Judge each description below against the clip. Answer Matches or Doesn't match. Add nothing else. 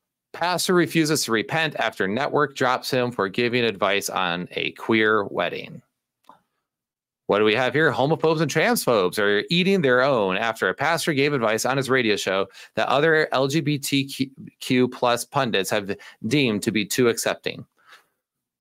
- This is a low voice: Matches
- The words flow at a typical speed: Matches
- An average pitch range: Doesn't match